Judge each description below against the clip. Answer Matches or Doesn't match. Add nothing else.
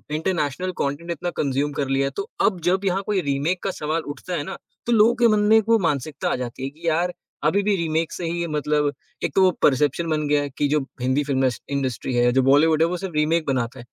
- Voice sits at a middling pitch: Matches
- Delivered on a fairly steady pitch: Doesn't match